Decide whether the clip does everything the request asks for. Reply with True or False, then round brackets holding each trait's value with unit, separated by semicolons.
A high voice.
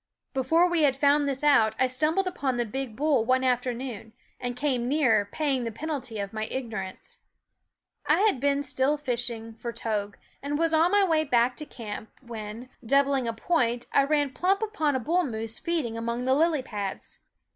True (260 Hz)